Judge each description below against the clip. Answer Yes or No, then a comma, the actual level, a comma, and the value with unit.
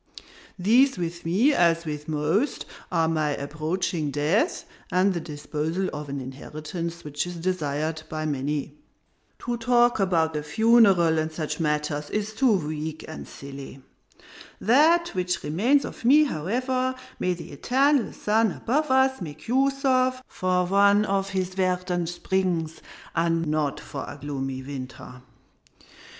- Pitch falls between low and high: Yes, medium, 175 Hz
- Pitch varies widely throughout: Yes, wide, 6.6 semitones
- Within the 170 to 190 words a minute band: No, slow, 135 wpm